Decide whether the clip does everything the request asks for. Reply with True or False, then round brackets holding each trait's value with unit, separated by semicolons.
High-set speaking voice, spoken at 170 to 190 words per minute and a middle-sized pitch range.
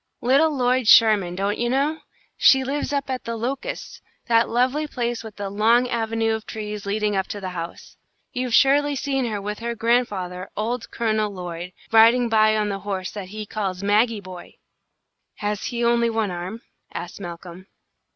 True (220 Hz; 175 wpm; 3.4 semitones)